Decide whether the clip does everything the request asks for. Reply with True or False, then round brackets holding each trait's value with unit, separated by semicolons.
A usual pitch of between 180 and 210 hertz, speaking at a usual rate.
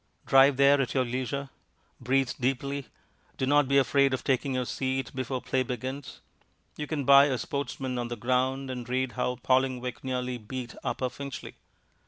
False (130 Hz; 170 wpm)